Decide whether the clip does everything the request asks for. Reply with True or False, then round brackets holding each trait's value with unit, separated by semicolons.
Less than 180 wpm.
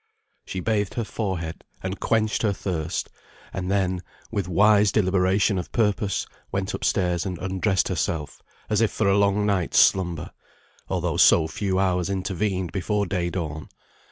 True (150 wpm)